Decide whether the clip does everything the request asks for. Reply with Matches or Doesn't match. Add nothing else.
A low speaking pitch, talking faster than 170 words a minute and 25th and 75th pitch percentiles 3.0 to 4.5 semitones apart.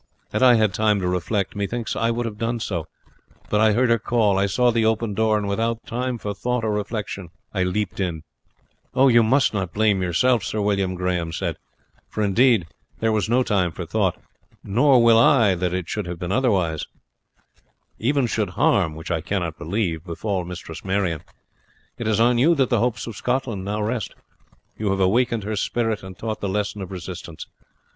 Matches